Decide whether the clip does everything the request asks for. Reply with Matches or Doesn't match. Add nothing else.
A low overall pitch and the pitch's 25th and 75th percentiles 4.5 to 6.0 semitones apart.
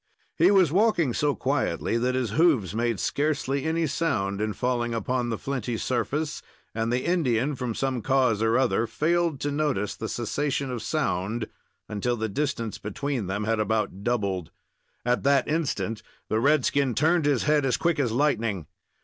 Matches